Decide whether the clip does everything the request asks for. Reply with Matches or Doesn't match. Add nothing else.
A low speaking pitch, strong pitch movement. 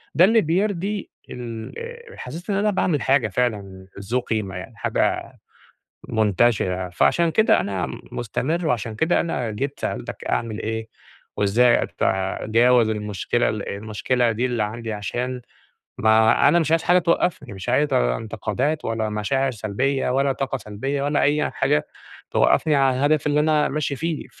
Matches